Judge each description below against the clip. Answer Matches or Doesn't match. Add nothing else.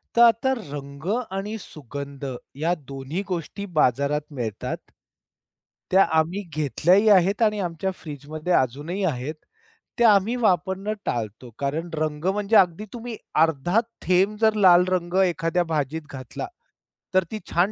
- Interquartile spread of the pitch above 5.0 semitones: Matches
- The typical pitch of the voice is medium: Matches